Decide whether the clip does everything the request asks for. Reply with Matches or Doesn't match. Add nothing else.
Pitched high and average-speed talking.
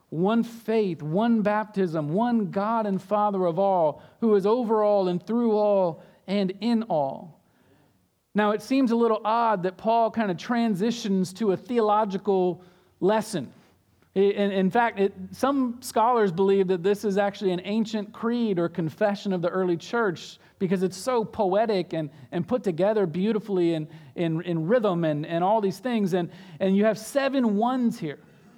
Matches